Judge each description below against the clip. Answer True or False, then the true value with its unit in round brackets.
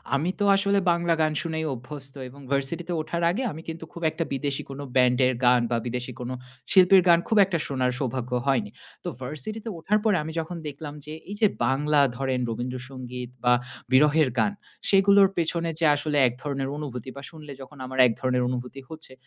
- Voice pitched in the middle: True (145 Hz)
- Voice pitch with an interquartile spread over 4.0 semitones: True (4.7 semitones)